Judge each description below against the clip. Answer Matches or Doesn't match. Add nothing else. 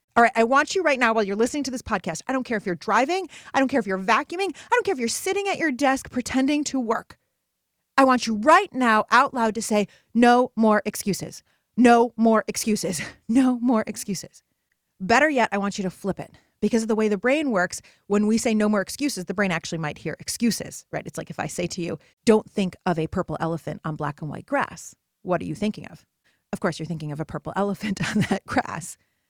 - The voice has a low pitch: Doesn't match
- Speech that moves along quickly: Matches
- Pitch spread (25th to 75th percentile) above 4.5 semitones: Matches